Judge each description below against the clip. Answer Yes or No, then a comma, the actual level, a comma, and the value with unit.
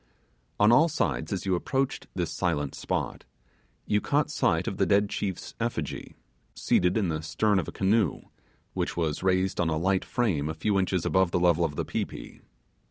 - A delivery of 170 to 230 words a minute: Yes, average, 190 wpm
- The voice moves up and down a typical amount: Yes, average, 3.9 semitones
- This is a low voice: Yes, very low, 95 Hz